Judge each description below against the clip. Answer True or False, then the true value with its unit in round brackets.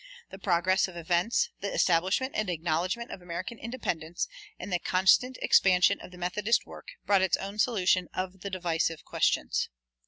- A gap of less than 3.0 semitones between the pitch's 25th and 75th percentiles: True (2.5 semitones)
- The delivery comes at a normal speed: True (160 wpm)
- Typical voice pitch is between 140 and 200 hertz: True (185 Hz)